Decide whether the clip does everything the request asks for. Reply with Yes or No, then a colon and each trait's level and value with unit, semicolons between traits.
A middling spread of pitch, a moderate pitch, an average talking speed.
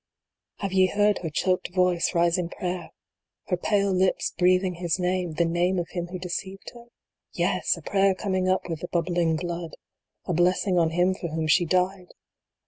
No: narrow, 1.5 semitones; medium, 180 Hz; average, 190 wpm